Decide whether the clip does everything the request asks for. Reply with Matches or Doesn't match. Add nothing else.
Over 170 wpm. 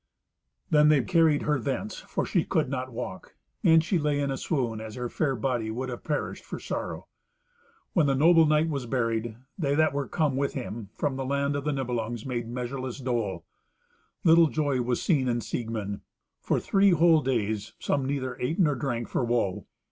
Matches